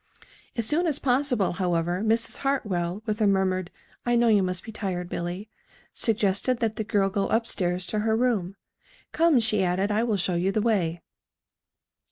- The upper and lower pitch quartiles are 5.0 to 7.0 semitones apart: No, average, 3.9 semitones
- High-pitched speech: Yes, high, 205 Hz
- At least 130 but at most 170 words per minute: No, average, 180 wpm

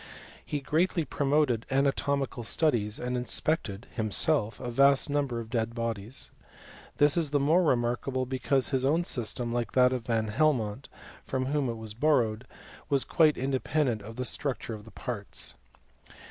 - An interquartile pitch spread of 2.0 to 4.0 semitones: Yes, average, 3.7 semitones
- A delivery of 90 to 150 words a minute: No, average, 160 wpm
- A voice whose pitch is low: Yes, low, 130 Hz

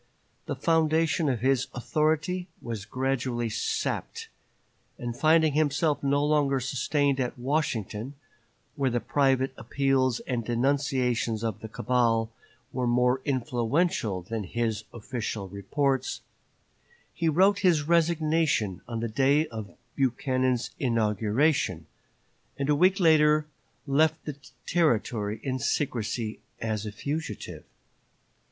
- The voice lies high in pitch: No, low, 130 Hz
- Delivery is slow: Yes, slow, 115 wpm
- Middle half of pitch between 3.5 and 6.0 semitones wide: Yes, average, 4.7 semitones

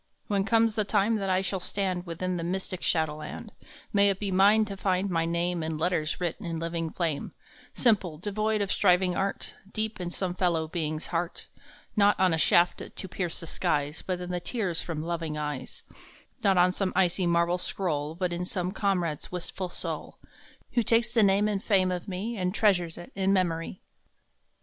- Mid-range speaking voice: Yes, medium, 180 Hz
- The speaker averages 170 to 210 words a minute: Yes, average, 190 wpm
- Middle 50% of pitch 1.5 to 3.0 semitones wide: Yes, average, 2.7 semitones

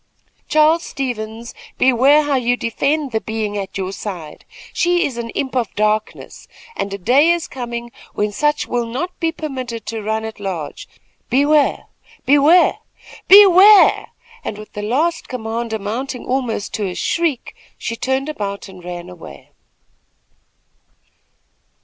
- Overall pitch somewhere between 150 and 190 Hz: No, high, 240 Hz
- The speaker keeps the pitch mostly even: No, wide, 5.5 semitones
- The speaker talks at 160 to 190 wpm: No, average, 140 wpm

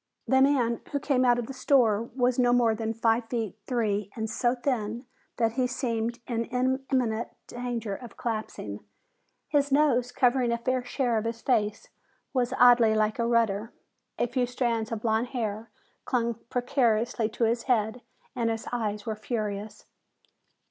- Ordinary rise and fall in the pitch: No, narrow, 2.1 semitones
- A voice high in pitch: Yes, high, 235 Hz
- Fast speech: No, average, 160 wpm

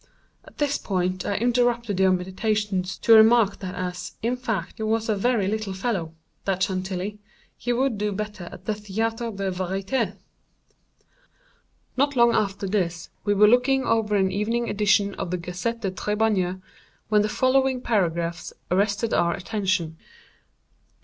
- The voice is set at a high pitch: Yes, high, 205 Hz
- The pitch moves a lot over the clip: No, average, 3.3 semitones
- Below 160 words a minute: Yes, average, 145 wpm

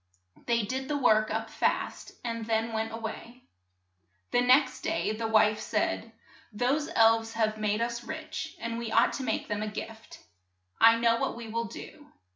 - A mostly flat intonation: Yes, narrow, 1.8 semitones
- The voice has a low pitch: No, high, 230 Hz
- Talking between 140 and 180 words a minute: No, average, 190 wpm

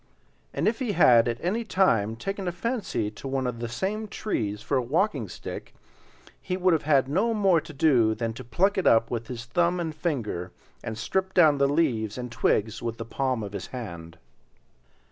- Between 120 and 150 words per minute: No, average, 200 wpm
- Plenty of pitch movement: Yes, wide, 7.9 semitones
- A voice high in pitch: No, low, 135 Hz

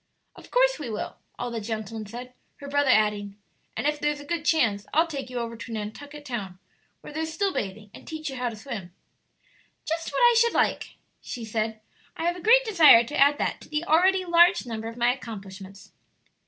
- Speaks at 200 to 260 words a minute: Yes, fast, 205 wpm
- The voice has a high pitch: Yes, very high, 250 Hz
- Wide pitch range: Yes, wide, 6.5 semitones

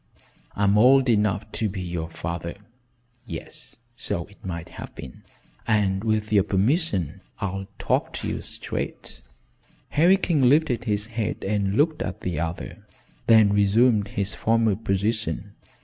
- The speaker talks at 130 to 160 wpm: Yes, average, 140 wpm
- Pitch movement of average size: Yes, average, 3.1 semitones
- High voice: No, low, 105 Hz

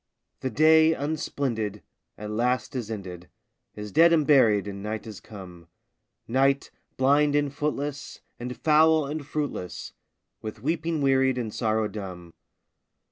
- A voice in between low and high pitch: No, low, 130 Hz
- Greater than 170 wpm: No, slow, 135 wpm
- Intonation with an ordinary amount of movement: No, wide, 5.7 semitones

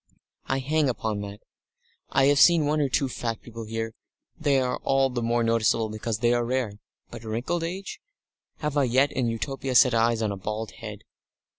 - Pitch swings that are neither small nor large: Yes, average, 3.4 semitones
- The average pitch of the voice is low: Yes, low, 120 Hz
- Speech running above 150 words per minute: Yes, average, 190 wpm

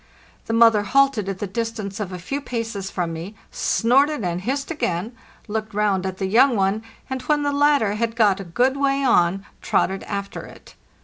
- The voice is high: Yes, high, 215 Hz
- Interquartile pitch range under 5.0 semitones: No, average, 5.3 semitones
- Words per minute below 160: No, average, 195 wpm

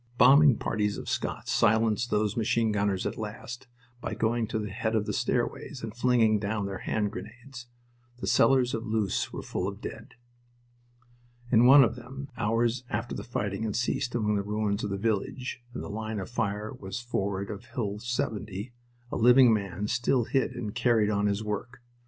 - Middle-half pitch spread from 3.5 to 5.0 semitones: No, narrow, 2.6 semitones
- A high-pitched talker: No, low, 110 Hz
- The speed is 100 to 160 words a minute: No, average, 185 wpm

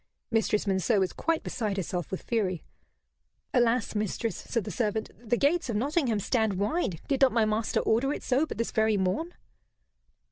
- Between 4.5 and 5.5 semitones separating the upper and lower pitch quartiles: No, average, 3.7 semitones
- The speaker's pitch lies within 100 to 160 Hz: No, high, 225 Hz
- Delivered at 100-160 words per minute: No, average, 175 wpm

